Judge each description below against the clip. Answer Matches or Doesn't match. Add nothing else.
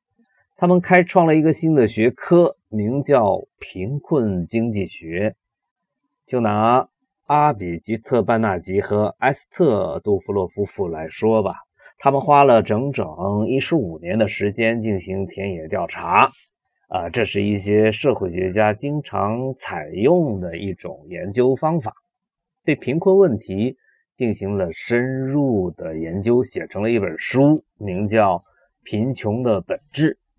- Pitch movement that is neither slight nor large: Doesn't match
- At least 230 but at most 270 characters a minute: Doesn't match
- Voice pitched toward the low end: Matches